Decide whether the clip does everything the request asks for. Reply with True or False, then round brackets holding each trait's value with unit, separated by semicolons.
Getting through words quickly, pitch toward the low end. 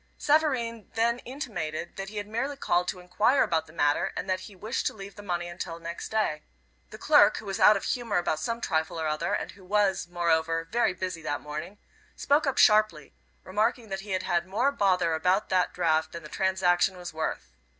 False (210 wpm; 185 Hz)